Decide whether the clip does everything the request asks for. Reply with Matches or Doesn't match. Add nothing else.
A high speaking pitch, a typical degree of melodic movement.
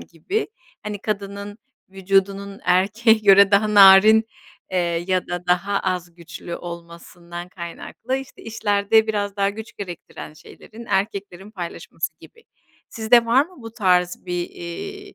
Matches